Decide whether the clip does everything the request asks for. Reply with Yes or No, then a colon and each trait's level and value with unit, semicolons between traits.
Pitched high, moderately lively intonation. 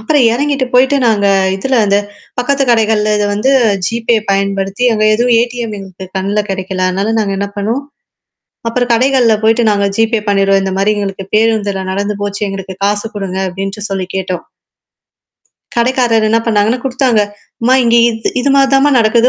Yes: high, 215 Hz; average, 3.4 semitones